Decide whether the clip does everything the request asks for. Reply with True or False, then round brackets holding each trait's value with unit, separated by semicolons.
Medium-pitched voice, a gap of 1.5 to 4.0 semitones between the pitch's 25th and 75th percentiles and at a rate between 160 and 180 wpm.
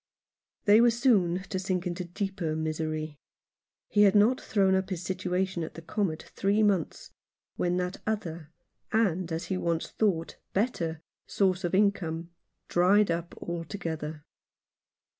False (180 Hz; 3.2 semitones; 150 wpm)